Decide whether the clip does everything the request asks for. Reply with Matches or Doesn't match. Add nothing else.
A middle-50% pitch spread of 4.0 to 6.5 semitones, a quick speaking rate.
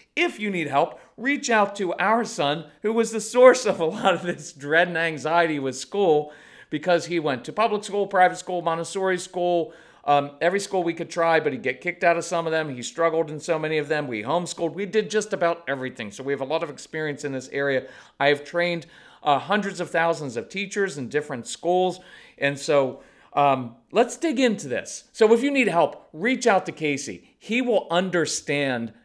Matches